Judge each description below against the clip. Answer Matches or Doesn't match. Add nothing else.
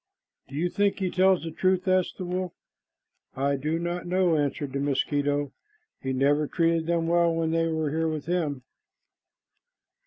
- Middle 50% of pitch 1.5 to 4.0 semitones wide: Matches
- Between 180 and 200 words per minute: Doesn't match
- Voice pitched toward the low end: Doesn't match